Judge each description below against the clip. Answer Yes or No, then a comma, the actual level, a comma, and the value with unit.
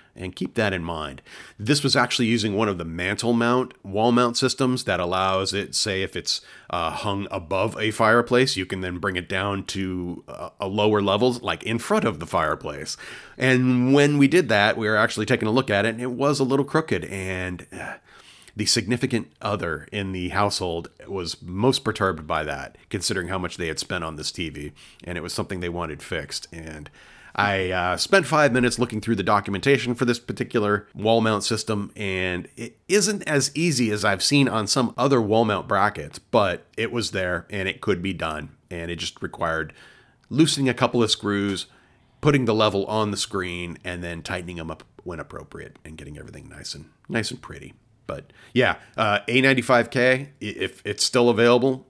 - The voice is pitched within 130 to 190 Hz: No, low, 105 Hz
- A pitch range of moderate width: Yes, average, 5.0 semitones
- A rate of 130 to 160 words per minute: No, average, 195 wpm